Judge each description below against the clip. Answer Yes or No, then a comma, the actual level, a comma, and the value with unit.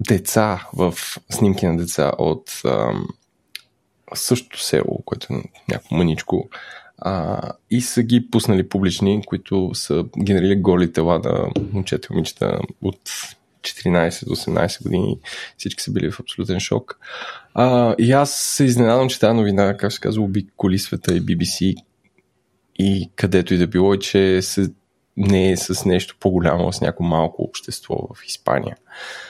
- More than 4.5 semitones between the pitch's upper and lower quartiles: No, average, 3.0 semitones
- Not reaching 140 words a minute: No, average, 145 wpm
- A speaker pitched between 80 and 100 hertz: Yes, very low, 95 Hz